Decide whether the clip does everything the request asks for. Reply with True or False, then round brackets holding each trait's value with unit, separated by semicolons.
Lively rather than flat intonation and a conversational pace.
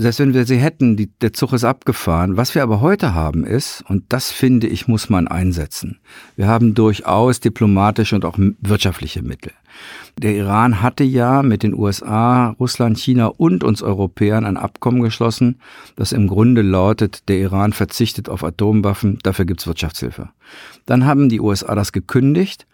False (3.7 semitones; 175 wpm)